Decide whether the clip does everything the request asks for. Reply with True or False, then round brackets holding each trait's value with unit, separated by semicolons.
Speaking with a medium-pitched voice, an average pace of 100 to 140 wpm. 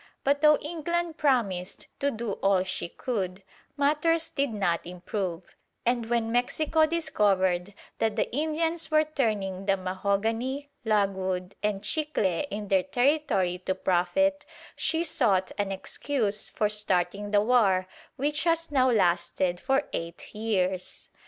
False (215 Hz; 135 wpm)